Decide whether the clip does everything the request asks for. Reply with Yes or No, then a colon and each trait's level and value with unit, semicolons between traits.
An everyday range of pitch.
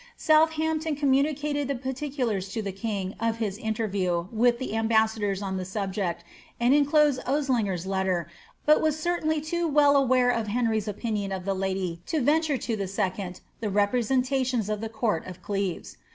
No: wide, 6.2 semitones